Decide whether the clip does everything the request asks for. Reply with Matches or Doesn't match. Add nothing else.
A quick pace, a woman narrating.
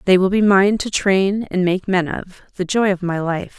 Matches